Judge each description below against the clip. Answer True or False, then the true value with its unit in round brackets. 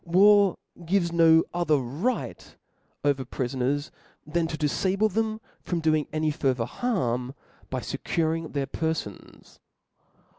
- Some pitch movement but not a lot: True (4.2 semitones)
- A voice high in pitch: False (160 Hz)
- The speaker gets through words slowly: True (115 wpm)